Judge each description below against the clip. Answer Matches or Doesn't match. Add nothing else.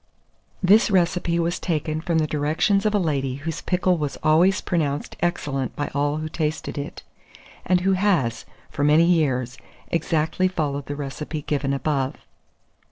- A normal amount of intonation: Matches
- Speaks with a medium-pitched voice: Matches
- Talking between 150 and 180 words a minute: Matches